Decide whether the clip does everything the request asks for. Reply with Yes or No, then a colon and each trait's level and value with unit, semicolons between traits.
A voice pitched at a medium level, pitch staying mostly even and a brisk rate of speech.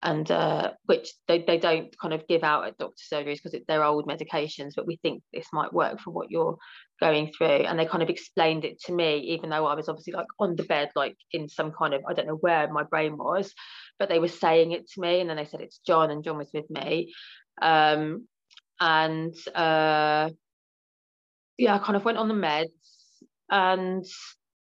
Yes: medium, 160 Hz; narrow, 2.2 semitones; fast, 215 wpm